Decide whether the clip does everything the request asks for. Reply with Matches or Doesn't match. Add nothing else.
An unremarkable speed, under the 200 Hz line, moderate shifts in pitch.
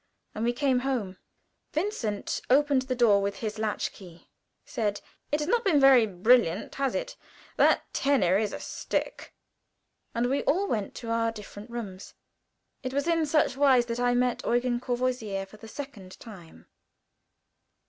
Doesn't match